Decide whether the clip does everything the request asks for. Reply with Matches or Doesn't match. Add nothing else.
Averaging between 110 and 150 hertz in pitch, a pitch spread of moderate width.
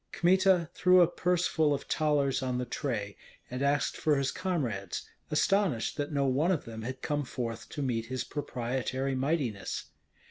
Matches